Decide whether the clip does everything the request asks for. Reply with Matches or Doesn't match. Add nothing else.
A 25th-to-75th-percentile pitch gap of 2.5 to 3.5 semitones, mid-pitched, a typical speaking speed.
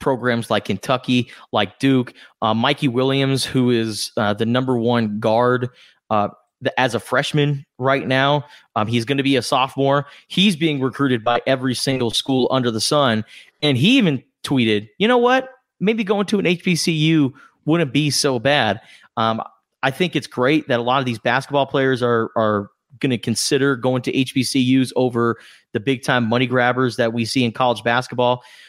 Doesn't match